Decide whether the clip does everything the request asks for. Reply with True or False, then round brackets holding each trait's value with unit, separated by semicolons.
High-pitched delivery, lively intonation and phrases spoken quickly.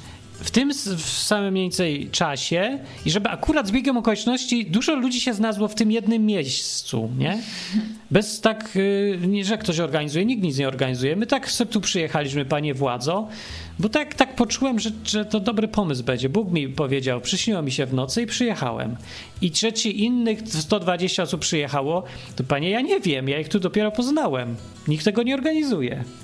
True (195 Hz; 7.1 semitones; 175 wpm)